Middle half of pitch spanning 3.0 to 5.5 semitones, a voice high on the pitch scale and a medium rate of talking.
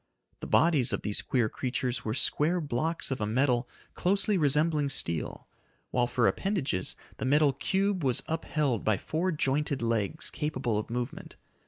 No: average, 4.7 semitones; medium, 140 Hz; average, 155 wpm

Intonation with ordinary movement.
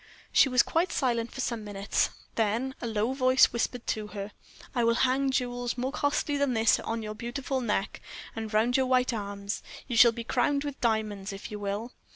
Yes: average, 3.3 semitones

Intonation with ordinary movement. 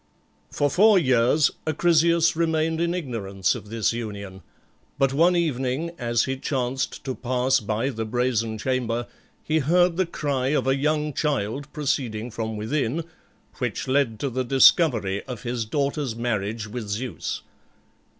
Yes: average, 4.9 semitones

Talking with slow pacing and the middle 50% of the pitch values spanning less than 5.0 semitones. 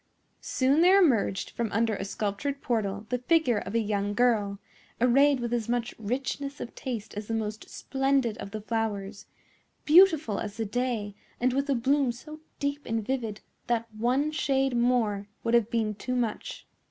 No: average, 175 wpm; average, 3.9 semitones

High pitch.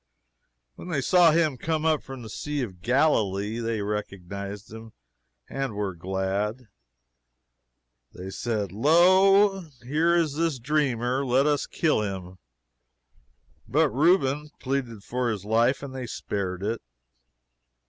No: low, 125 Hz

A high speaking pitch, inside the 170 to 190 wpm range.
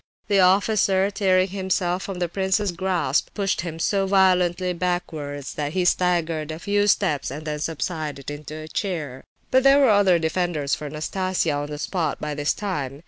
No: medium, 175 Hz; average, 175 wpm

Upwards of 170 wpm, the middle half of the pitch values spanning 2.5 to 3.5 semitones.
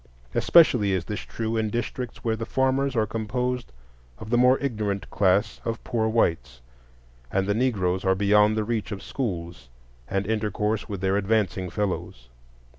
No: average, 160 wpm; average, 3.2 semitones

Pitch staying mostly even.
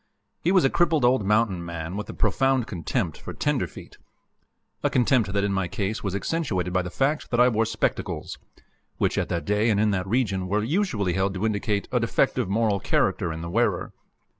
No: average, 4.3 semitones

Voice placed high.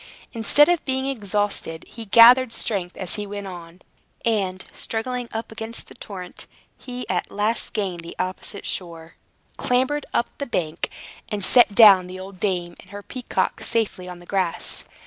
Yes: high, 205 Hz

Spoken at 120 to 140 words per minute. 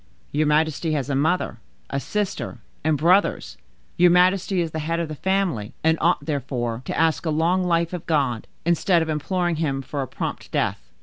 No: average, 190 wpm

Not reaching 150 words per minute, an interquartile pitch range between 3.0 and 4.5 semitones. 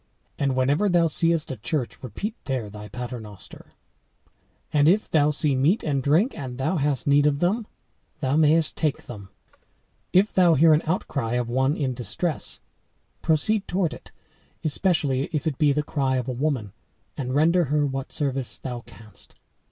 No: average, 165 wpm; average, 3.9 semitones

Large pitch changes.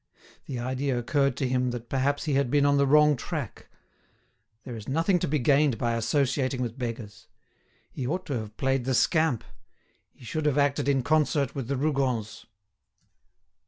No: average, 2.8 semitones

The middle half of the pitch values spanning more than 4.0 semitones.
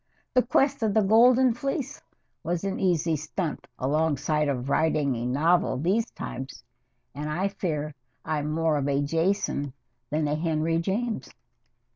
Yes: average, 5.1 semitones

